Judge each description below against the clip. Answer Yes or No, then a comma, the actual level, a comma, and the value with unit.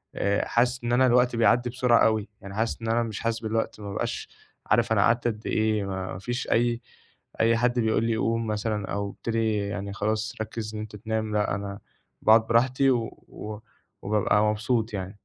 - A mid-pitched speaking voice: No, low, 110 Hz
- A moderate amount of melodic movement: No, narrow, 1.9 semitones